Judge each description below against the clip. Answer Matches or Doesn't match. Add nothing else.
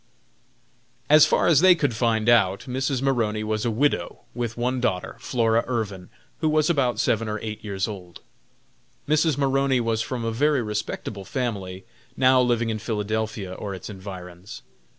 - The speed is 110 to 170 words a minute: Matches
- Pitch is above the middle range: Doesn't match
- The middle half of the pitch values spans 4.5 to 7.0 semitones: Doesn't match